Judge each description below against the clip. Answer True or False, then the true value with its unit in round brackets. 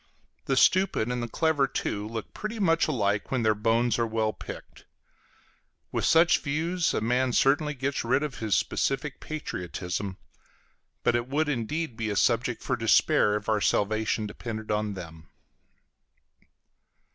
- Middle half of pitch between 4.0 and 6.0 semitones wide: True (5.6 semitones)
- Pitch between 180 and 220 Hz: False (120 Hz)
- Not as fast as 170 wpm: True (150 wpm)